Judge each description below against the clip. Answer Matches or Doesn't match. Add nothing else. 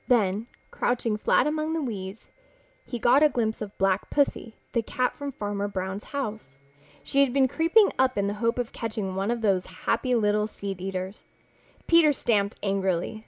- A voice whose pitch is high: Matches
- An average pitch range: Matches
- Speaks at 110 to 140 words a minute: Doesn't match